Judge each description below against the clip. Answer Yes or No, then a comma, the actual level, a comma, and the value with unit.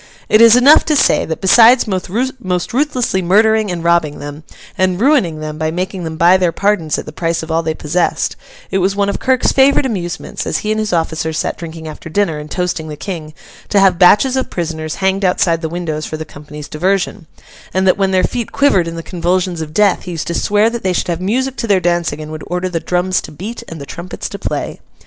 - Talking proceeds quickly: Yes, fast, 230 wpm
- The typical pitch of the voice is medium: Yes, medium, 180 Hz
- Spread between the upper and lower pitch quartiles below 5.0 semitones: Yes, average, 4.0 semitones